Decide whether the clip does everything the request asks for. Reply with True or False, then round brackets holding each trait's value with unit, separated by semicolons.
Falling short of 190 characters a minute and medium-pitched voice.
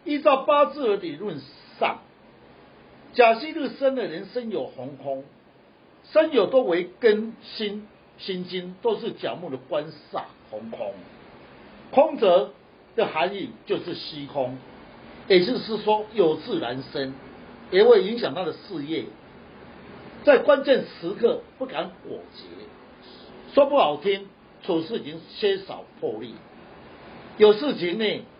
False (180 characters per minute; 220 Hz)